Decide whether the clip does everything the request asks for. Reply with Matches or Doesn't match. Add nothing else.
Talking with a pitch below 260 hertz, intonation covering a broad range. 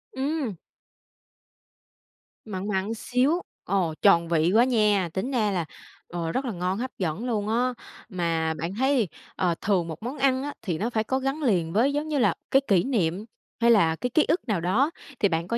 Matches